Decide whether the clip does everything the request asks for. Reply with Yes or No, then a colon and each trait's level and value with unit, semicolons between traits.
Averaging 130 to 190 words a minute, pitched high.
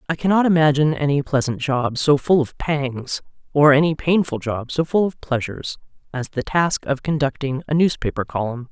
No: average, 185 wpm; medium, 145 Hz